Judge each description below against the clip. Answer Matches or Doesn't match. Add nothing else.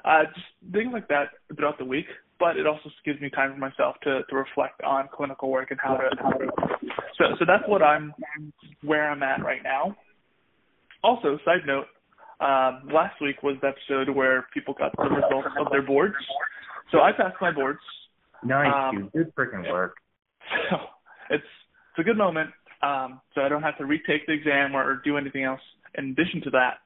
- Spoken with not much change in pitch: Matches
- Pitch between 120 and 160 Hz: Matches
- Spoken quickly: Doesn't match